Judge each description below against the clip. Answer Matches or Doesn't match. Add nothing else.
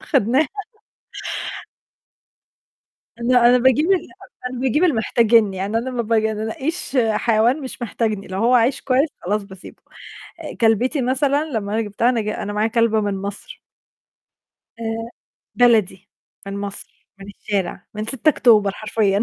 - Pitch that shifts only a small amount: Doesn't match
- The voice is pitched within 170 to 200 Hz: Doesn't match